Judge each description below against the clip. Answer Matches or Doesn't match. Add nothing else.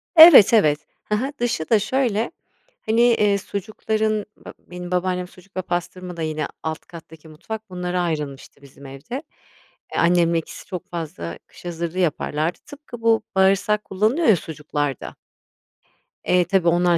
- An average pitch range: Matches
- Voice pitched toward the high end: Doesn't match